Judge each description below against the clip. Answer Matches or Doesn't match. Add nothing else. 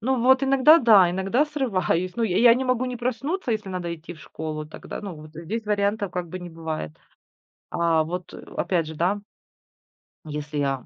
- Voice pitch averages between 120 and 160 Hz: Doesn't match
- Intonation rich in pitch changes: Matches